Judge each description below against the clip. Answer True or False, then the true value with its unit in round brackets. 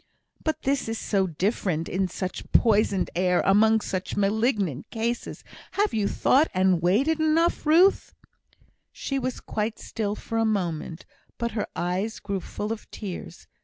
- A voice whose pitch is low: False (210 Hz)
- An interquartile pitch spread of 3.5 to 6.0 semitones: True (4.1 semitones)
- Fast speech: False (155 wpm)